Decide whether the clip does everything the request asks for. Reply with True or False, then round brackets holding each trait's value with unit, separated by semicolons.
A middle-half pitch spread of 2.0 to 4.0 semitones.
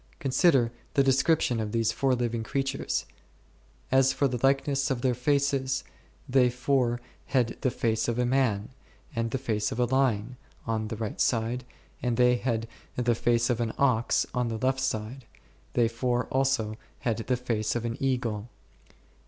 True (2.5 semitones)